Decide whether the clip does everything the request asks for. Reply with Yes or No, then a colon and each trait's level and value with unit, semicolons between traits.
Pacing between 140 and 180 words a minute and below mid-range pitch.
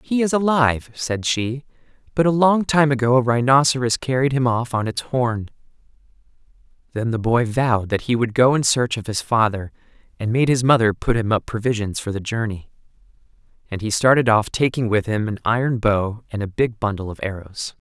No: average, 195 wpm; low, 120 Hz